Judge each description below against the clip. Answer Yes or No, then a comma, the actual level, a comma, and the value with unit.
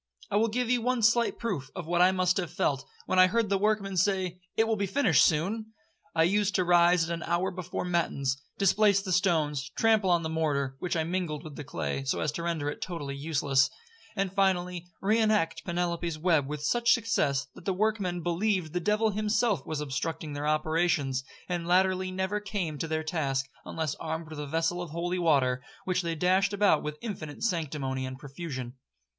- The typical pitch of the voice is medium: Yes, medium, 175 Hz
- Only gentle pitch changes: No, average, 4.2 semitones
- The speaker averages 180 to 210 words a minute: Yes, average, 200 wpm